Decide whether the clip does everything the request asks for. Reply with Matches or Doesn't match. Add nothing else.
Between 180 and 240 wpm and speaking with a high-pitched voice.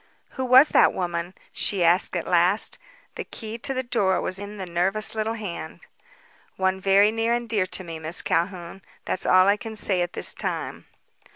Matches